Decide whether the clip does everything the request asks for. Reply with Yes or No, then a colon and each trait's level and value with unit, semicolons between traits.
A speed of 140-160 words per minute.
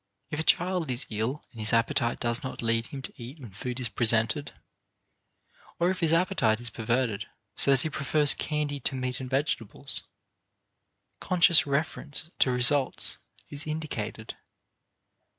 Yes: average, 150 wpm